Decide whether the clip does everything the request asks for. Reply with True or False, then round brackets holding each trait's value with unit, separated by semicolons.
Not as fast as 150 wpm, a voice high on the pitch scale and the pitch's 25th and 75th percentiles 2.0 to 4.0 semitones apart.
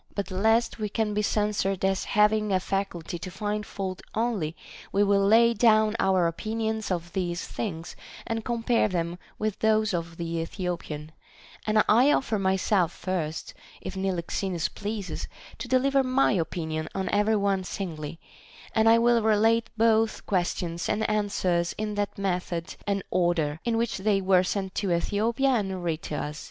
False (160 wpm; 200 Hz; 3.7 semitones)